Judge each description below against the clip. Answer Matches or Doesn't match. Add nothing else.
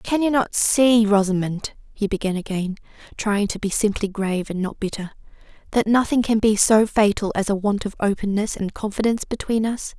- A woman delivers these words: Matches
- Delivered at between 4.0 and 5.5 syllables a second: Matches